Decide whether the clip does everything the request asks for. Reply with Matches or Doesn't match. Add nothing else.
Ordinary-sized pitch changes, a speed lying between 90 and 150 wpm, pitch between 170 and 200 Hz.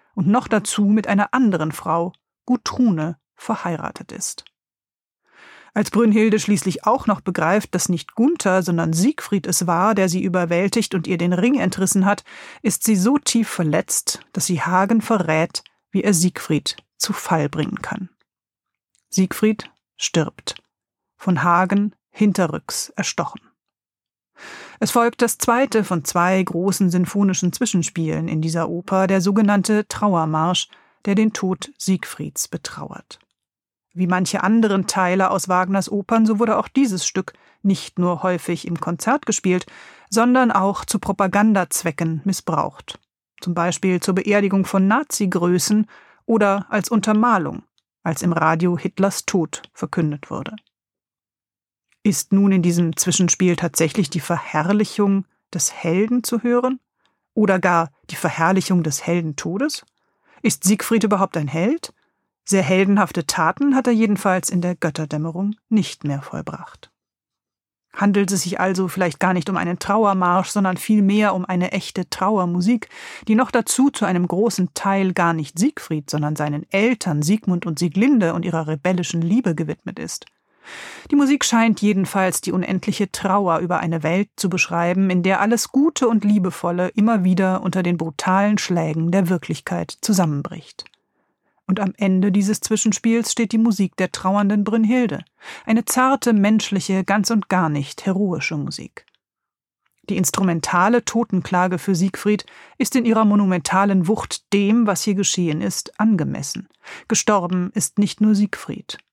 Matches